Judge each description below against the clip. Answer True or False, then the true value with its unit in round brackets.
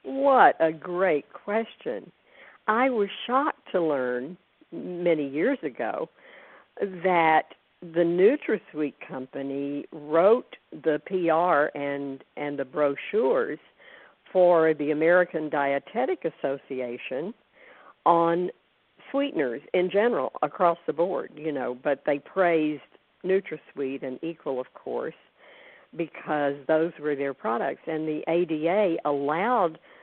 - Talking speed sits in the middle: False (110 wpm)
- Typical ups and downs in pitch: True (3.9 semitones)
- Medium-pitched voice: True (160 Hz)